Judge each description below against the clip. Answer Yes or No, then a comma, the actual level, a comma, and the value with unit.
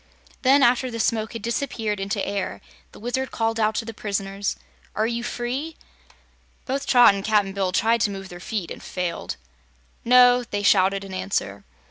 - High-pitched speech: Yes, high, 215 Hz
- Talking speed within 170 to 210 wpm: Yes, average, 175 wpm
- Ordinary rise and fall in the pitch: Yes, average, 3.5 semitones